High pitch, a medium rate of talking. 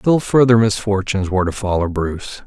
No: low, 105 Hz; average, 170 wpm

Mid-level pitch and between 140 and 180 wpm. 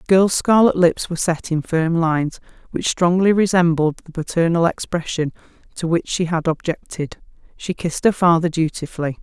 Yes: medium, 170 Hz; average, 165 wpm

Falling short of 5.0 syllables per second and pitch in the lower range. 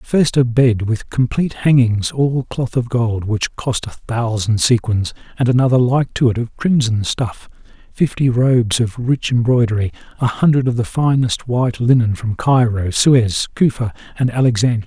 Yes: 4.7 syllables/s; low, 120 Hz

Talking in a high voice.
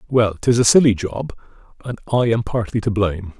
No: low, 110 Hz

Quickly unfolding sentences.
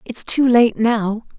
No: average, 175 wpm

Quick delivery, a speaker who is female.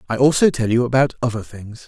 No: fast, 225 wpm; male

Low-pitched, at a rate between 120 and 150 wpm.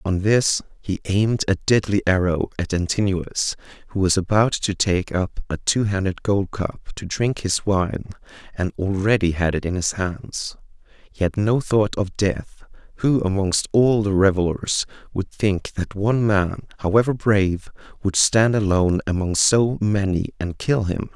No: low, 100 Hz; average, 160 wpm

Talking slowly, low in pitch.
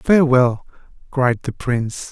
Yes: slow, 115 wpm; low, 130 Hz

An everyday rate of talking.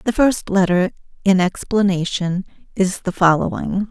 No: slow, 125 wpm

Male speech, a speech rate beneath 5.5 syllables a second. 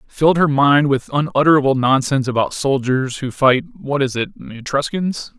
Yes: male; 5.1 syllables/s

